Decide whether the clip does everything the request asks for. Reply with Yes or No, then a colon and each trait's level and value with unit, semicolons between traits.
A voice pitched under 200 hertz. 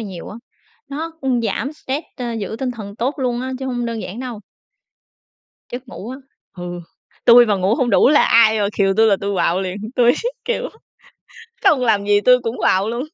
No: high, 235 Hz